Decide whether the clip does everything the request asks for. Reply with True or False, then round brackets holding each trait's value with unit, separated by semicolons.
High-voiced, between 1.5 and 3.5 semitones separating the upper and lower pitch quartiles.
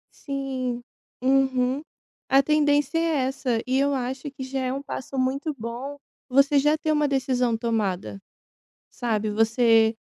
True (260 Hz; 2.6 semitones)